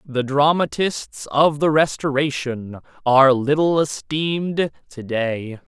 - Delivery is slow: Yes, slow, 105 wpm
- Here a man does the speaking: Yes, male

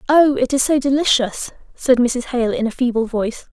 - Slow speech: No, fast, 205 wpm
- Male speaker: No, female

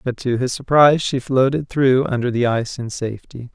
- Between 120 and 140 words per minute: No, fast, 205 wpm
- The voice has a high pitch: No, low, 130 Hz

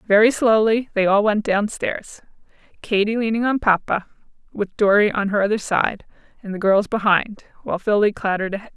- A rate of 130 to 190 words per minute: Yes, average, 170 wpm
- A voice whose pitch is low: No, high, 210 Hz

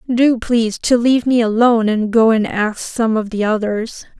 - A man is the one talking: No, female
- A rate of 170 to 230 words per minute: Yes, average, 200 wpm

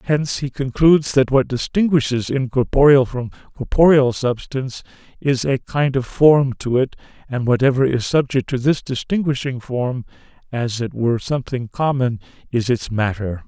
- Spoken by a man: Yes, male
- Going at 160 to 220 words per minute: No, average, 145 wpm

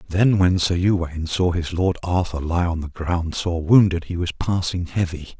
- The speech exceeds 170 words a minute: Yes, average, 200 wpm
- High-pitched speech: No, very low, 85 Hz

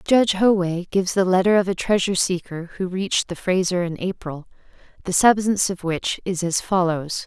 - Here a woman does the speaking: Yes, female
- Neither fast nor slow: Yes, average, 180 wpm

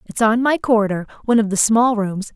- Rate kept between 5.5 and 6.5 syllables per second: Yes, 5.8 syllables/s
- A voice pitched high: Yes, high, 220 Hz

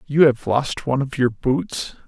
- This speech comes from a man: Yes, male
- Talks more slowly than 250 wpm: Yes, average, 200 wpm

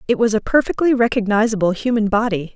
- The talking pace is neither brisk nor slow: Yes, average, 165 wpm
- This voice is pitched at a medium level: No, high, 220 Hz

